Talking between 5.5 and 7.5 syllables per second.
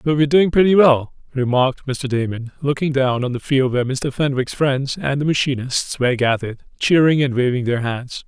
Yes: 5.7 syllables/s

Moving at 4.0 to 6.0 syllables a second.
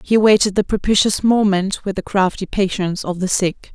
Yes: 5.5 syllables/s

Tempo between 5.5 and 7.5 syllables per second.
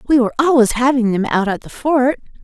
Yes: 6.0 syllables/s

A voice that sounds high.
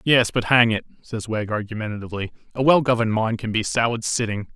No: low, 115 Hz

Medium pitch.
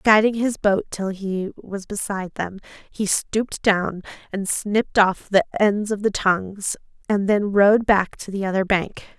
No: high, 200 Hz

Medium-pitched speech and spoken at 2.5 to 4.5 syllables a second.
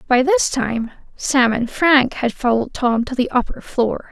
No: very high, 255 Hz; 4.3 syllables/s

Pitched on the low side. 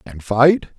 Yes: low, 125 Hz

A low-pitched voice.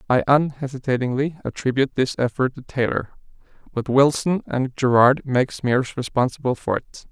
Yes: low, 130 Hz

